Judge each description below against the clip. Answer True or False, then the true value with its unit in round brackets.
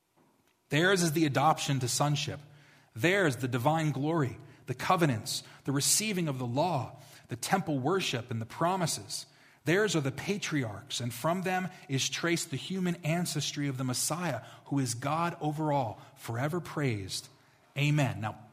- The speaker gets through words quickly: False (150 wpm)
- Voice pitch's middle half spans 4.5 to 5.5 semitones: False (3.6 semitones)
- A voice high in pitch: False (145 Hz)